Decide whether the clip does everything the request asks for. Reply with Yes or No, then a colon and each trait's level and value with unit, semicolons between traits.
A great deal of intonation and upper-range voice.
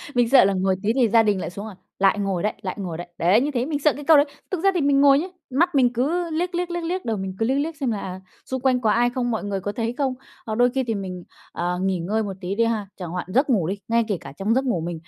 Yes: wide, 6.0 semitones; high, 230 Hz